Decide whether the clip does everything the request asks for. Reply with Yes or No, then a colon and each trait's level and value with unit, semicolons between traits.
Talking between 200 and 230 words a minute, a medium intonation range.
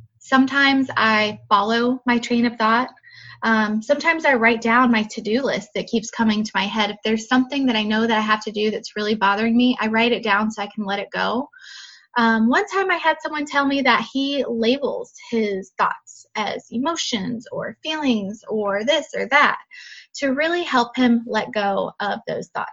Yes: fast, 205 wpm; average, 3.7 semitones